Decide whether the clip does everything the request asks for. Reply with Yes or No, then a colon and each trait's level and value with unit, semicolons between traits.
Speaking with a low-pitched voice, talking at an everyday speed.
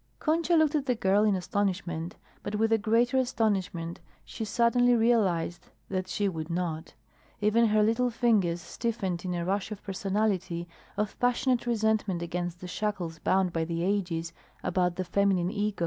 No: high, 200 Hz; average, 165 wpm